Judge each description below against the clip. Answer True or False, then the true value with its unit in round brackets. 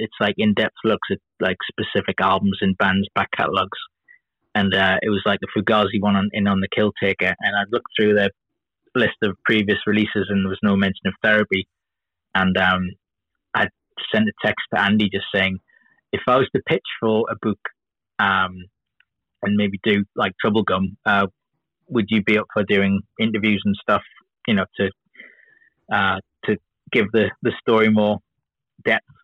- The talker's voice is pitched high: False (100 Hz)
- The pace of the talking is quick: False (180 wpm)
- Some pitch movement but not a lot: False (1.7 semitones)